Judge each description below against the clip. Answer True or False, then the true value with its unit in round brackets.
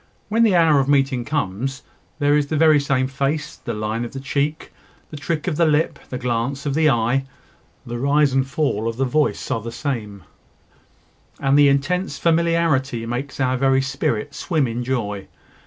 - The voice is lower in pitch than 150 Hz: True (135 Hz)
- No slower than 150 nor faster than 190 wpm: True (185 wpm)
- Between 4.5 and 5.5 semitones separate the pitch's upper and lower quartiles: False (3.5 semitones)